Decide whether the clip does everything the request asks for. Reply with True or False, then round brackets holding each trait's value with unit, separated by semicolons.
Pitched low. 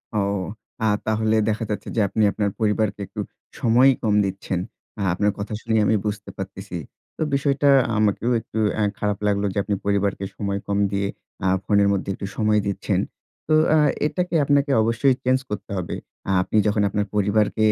True (105 Hz)